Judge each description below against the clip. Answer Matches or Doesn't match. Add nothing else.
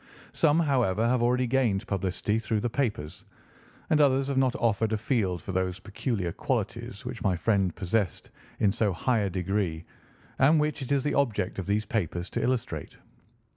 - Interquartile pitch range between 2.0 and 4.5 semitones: Doesn't match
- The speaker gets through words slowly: Doesn't match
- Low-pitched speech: Matches